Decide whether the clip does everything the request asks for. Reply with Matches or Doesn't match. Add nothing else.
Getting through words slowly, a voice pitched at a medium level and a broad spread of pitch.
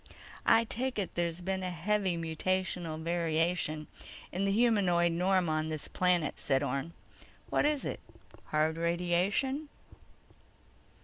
Doesn't match